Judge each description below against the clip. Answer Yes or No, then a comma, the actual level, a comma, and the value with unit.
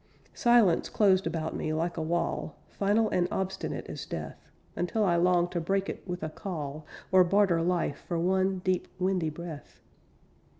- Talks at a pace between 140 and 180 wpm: Yes, average, 165 wpm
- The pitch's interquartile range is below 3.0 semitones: Yes, narrow, 2.5 semitones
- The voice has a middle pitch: Yes, medium, 180 Hz